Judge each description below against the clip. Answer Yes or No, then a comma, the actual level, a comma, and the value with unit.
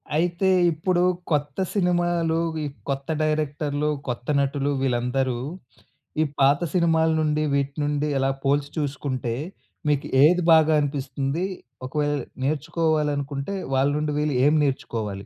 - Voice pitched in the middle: Yes, medium, 145 Hz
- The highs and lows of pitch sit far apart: No, narrow, 2.5 semitones